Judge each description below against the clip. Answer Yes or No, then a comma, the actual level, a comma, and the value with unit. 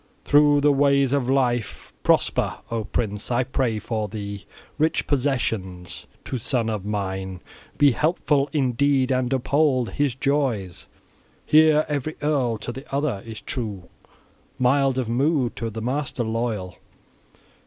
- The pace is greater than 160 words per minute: No, average, 140 wpm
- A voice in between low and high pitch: No, low, 125 Hz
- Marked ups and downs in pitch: No, average, 4.3 semitones